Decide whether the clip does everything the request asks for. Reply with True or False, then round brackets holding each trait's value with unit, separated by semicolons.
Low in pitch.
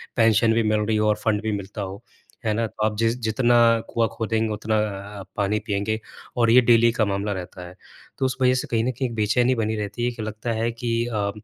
True (110 Hz)